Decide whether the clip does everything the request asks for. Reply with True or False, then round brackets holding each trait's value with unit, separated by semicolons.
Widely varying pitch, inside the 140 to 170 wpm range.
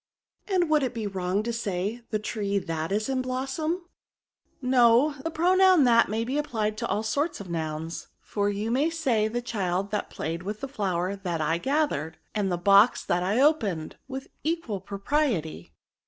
False (6.1 semitones; 190 wpm)